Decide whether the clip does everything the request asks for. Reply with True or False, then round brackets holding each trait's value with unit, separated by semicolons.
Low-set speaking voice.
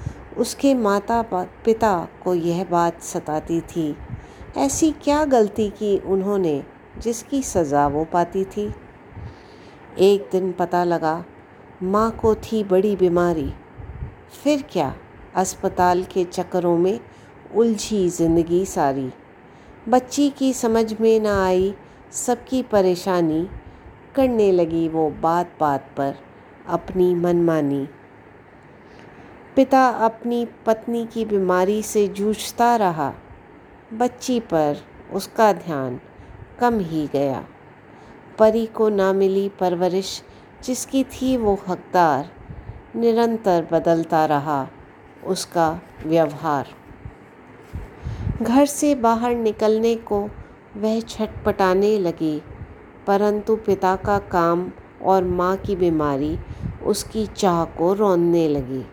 False (190 Hz)